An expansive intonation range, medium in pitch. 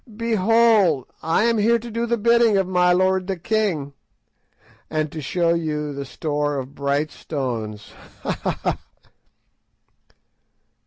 Yes: wide, 6.9 semitones; medium, 175 Hz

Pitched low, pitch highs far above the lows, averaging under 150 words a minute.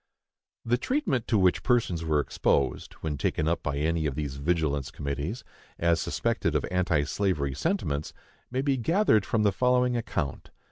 No: very low, 85 Hz; wide, 8.7 semitones; average, 160 wpm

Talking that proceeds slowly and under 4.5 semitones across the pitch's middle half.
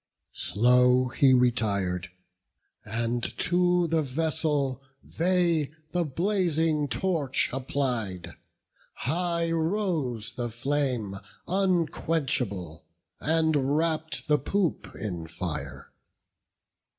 No: slow, 80 wpm; wide, 5.4 semitones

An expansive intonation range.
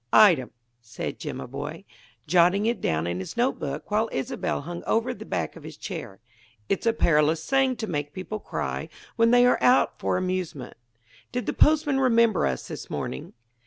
Yes: wide, 8.3 semitones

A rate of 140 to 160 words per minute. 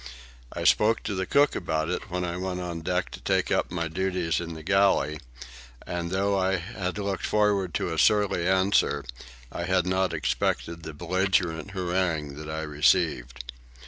No: average, 175 wpm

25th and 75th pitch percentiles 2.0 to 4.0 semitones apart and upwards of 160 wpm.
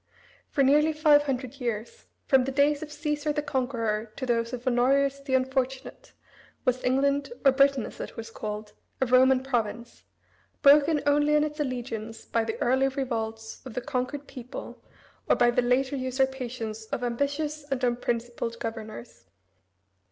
No: average, 3.0 semitones; average, 155 wpm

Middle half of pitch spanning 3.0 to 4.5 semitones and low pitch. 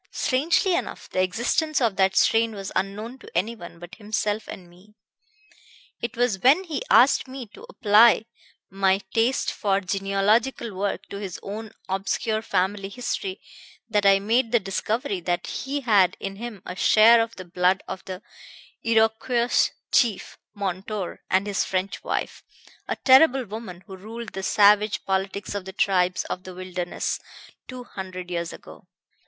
No: average, 3.4 semitones; high, 205 Hz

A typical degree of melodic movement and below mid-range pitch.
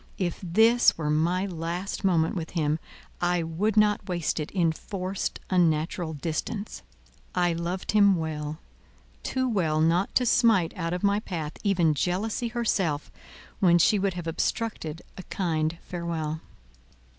No: average, 3.6 semitones; medium, 175 Hz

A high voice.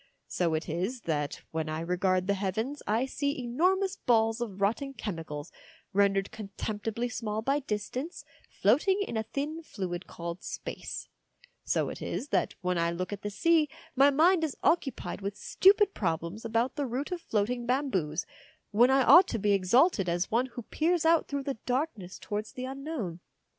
Yes: high, 225 Hz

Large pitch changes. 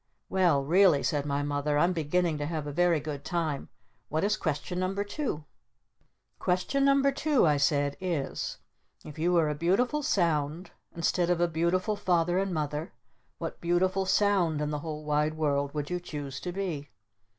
No: average, 3.7 semitones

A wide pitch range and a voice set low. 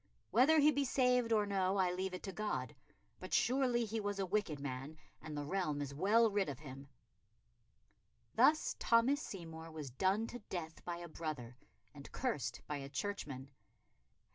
No: wide, 7.2 semitones; high, 190 Hz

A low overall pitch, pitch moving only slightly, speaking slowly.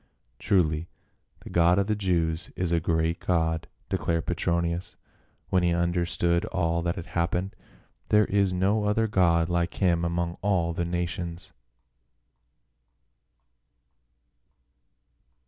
Yes: very low, 85 Hz; narrow, 1.6 semitones; slow, 125 wpm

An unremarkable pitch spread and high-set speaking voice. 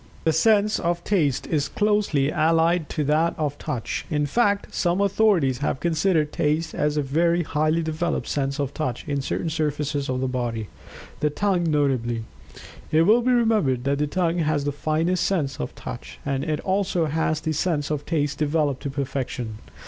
No: average, 3.4 semitones; medium, 155 Hz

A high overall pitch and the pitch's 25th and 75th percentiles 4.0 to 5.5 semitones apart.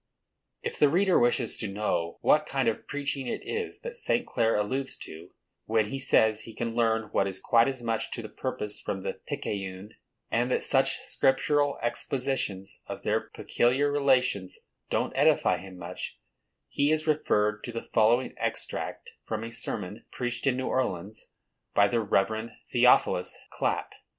No: low, 115 Hz; average, 4.3 semitones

